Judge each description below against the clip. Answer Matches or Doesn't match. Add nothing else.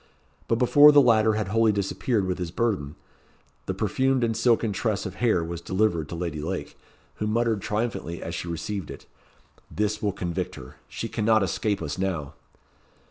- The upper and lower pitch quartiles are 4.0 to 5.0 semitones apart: Matches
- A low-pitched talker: Matches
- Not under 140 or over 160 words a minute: Doesn't match